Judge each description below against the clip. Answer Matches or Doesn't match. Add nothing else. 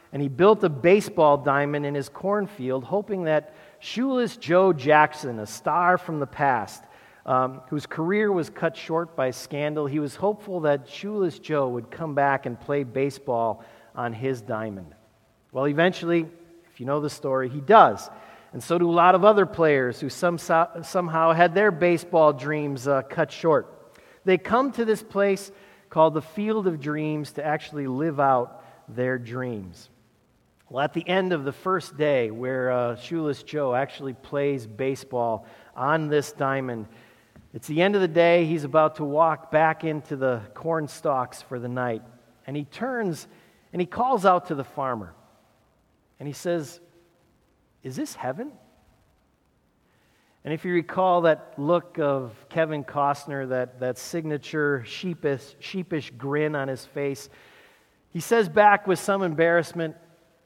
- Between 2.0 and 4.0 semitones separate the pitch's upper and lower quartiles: Doesn't match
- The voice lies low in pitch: Doesn't match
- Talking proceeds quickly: Doesn't match